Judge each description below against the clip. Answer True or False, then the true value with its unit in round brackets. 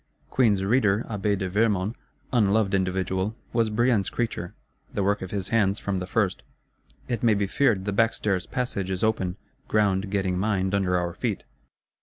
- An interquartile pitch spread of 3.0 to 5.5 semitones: False (2.6 semitones)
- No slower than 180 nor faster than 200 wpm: False (165 wpm)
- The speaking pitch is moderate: False (100 Hz)